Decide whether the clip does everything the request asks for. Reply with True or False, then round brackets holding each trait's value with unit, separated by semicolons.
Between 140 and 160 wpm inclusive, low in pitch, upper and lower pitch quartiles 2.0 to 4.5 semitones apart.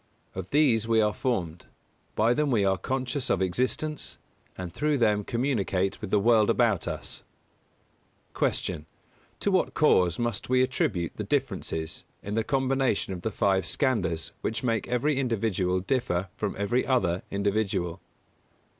False (150 wpm; 110 Hz; 5.2 semitones)